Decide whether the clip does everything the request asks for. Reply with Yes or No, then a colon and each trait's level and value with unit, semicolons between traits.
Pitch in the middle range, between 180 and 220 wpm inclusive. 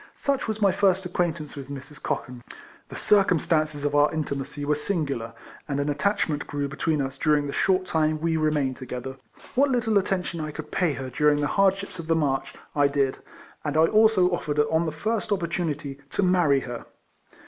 Yes: medium, 155 Hz; average, 185 wpm